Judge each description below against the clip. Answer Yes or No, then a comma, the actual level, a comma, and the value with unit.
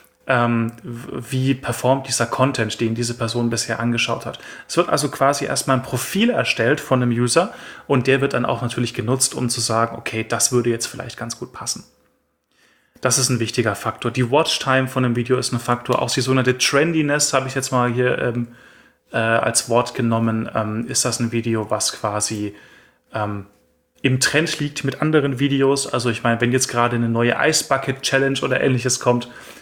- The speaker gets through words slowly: No, fast, 190 wpm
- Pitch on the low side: Yes, low, 125 Hz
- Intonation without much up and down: Yes, narrow, 2.3 semitones